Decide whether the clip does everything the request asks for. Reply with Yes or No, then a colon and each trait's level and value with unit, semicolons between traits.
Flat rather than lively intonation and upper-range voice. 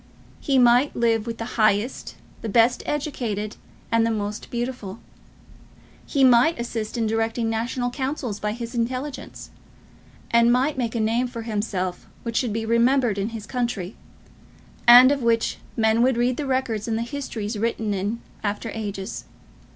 Yes: narrow, 2.1 semitones; high, 230 Hz